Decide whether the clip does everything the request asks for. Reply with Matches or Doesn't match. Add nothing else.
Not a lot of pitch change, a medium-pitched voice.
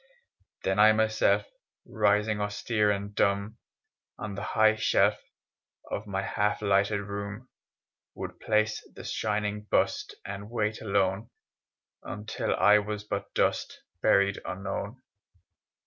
Doesn't match